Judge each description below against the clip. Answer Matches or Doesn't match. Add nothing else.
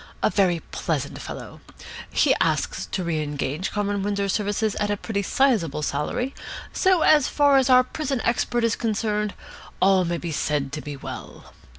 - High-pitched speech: Matches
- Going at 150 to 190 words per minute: Matches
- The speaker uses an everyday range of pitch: Doesn't match